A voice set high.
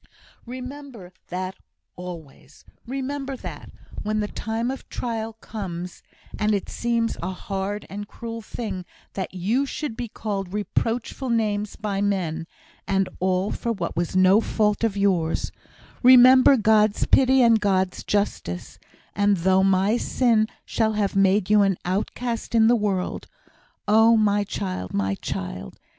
Yes: high, 210 Hz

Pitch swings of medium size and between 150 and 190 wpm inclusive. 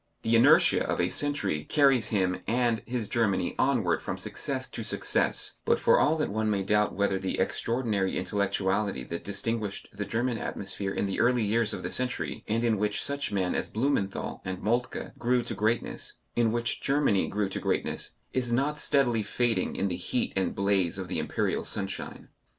Yes: average, 3.7 semitones; average, 185 wpm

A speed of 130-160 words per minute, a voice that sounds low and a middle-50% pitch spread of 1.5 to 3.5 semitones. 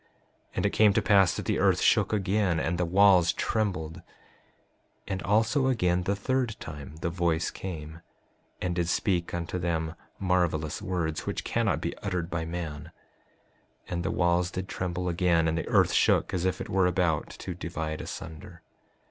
No: average, 175 wpm; very low, 90 Hz; narrow, 2.5 semitones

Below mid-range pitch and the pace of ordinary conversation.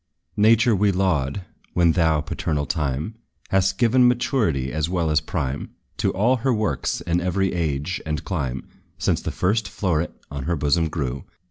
Yes: very low, 85 Hz; average, 160 wpm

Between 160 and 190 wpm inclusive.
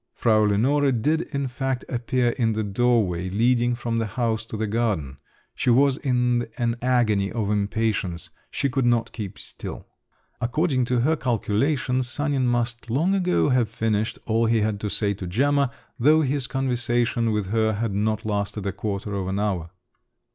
Yes: average, 170 wpm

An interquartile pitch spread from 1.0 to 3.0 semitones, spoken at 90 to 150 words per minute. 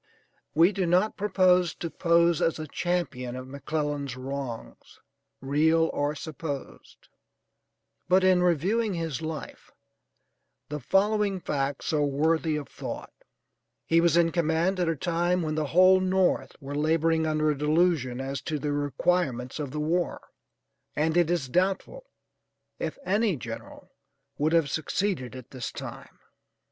No: average, 3.7 semitones; average, 140 wpm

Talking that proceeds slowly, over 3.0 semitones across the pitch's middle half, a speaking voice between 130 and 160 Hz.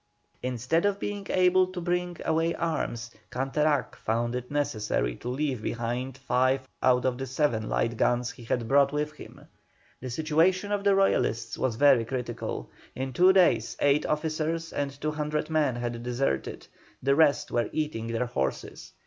No: average, 160 wpm; average, 4.6 semitones; low, 135 Hz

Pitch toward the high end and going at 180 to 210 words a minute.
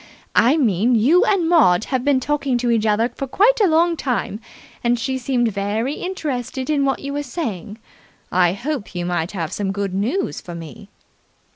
Yes: high, 245 Hz; average, 185 wpm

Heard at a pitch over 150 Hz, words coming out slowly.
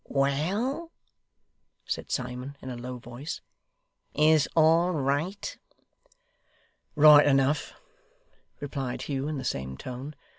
No: medium, 140 Hz; slow, 105 wpm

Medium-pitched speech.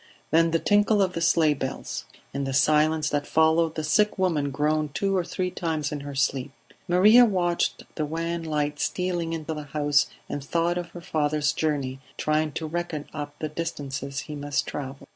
Yes: medium, 155 Hz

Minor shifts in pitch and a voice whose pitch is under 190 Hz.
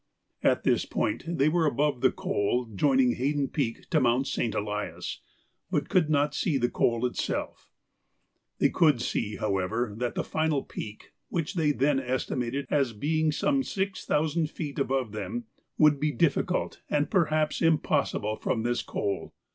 No: average, 4.4 semitones; medium, 140 Hz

